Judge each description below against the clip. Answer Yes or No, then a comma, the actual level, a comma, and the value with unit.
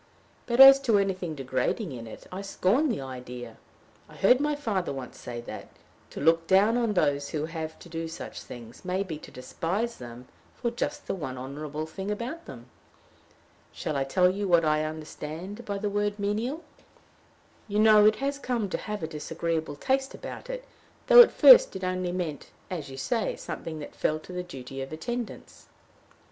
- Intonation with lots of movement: Yes, wide, 6.3 semitones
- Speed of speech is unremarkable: Yes, average, 185 wpm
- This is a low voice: No, medium, 180 Hz